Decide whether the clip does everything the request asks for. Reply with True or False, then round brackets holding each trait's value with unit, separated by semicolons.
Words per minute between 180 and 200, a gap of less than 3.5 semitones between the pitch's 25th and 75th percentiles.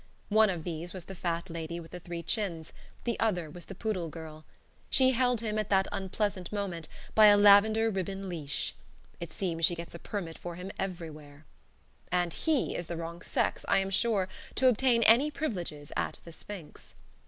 False (190 wpm; 4.0 semitones)